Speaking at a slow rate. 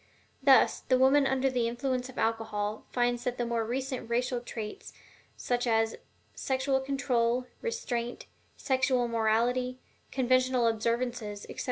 Yes: slow, 130 wpm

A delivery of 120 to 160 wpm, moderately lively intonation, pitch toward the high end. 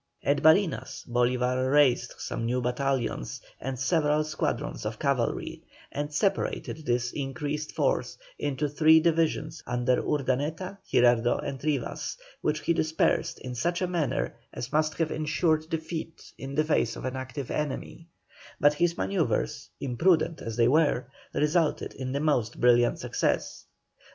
No: average, 140 wpm; average, 3.8 semitones; medium, 145 Hz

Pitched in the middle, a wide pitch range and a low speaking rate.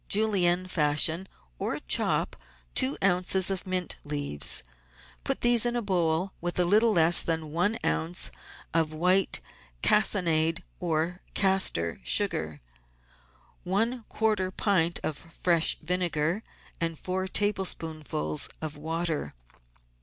No: medium, 175 Hz; average, 3.5 semitones; slow, 115 wpm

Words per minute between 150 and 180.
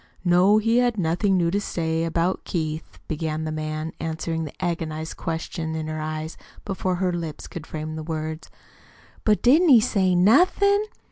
Yes: average, 165 wpm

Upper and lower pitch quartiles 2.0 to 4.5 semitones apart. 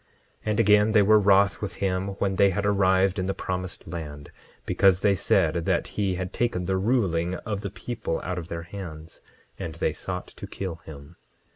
Yes: narrow, 2.6 semitones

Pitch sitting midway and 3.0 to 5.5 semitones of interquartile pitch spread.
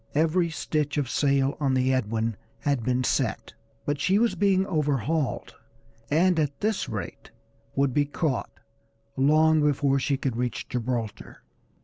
Yes: medium, 145 Hz; average, 3.4 semitones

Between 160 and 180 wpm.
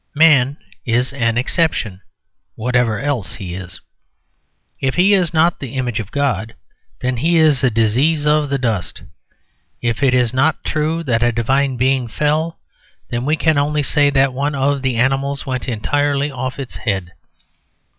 Yes: average, 165 wpm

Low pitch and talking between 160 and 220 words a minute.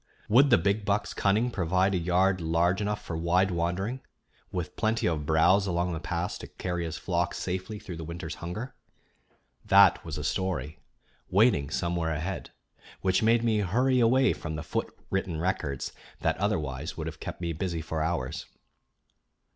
Yes: very low, 90 Hz; average, 170 wpm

